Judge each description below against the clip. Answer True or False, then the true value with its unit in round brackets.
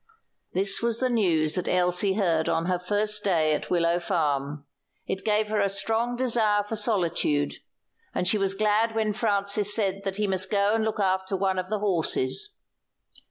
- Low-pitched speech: False (195 Hz)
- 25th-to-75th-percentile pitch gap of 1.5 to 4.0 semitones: True (3.1 semitones)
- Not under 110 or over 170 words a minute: False (180 wpm)